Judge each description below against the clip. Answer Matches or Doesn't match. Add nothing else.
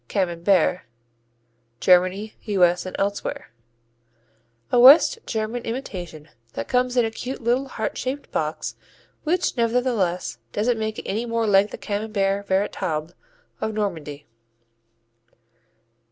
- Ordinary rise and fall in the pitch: Matches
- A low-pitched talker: Doesn't match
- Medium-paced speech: Doesn't match